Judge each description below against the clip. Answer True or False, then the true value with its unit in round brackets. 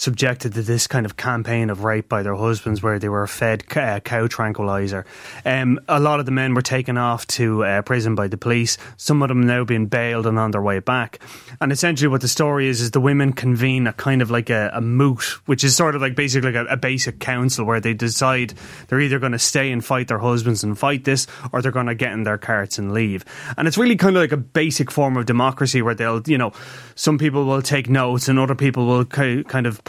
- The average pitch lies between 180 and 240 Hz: False (125 Hz)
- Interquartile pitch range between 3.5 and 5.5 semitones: False (2.9 semitones)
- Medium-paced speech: False (245 wpm)